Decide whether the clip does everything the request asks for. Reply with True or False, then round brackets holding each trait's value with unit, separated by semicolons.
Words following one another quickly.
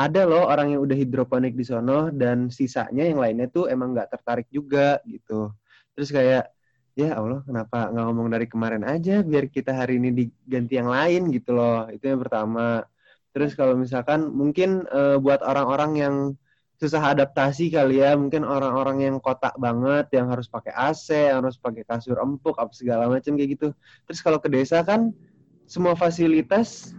True (175 wpm)